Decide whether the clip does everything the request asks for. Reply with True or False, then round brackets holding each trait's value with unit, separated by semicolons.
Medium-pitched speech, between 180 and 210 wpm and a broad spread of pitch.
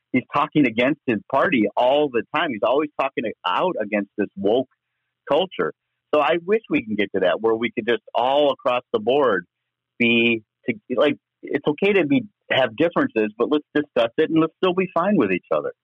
True (150 Hz; 200 wpm; 6.9 semitones)